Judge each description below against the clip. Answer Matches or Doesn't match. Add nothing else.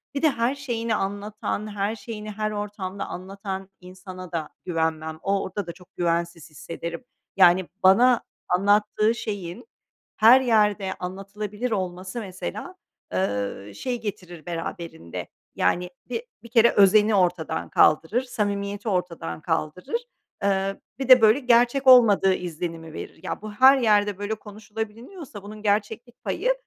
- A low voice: Doesn't match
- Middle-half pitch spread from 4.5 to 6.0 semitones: Doesn't match